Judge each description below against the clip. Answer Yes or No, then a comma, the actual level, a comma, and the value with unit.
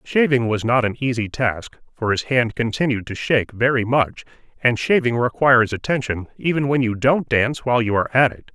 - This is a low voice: Yes, low, 120 Hz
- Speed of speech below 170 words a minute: No, average, 195 wpm